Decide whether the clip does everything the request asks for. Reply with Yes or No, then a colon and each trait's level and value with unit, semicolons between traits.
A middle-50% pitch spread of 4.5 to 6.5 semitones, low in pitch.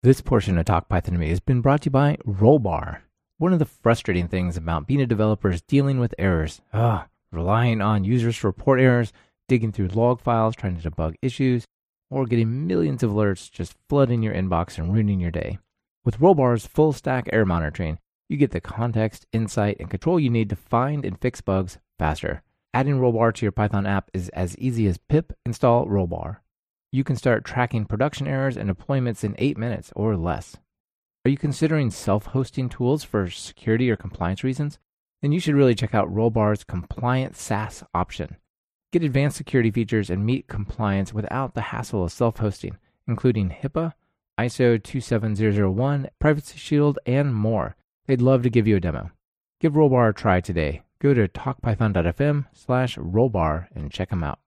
Yes: average, 5.1 semitones; low, 115 Hz